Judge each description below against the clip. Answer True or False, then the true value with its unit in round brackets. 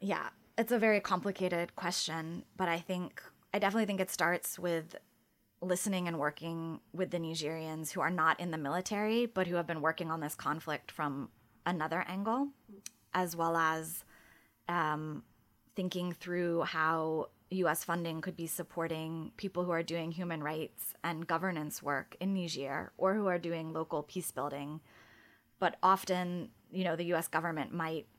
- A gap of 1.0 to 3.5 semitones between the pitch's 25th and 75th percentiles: True (2.6 semitones)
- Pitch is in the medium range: True (170 Hz)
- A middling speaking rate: True (160 wpm)